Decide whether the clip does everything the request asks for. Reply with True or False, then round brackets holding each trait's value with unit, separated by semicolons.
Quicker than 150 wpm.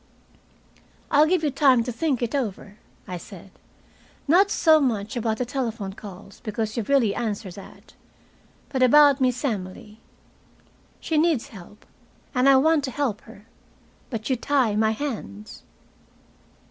False (145 wpm)